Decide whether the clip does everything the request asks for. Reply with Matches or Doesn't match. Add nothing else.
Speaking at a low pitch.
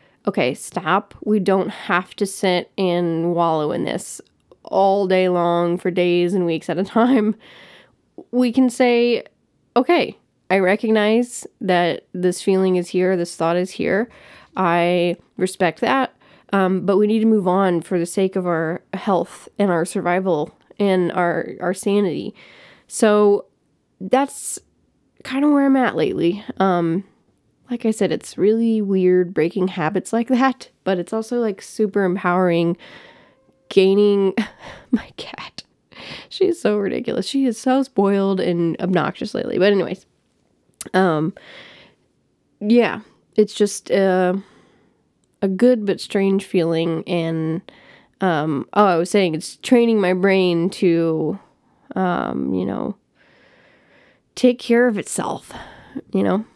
Doesn't match